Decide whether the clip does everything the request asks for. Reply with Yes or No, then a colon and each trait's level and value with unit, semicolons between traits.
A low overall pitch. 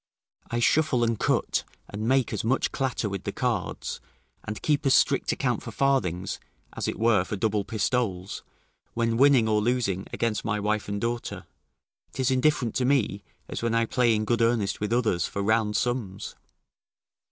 Yes: low, 115 Hz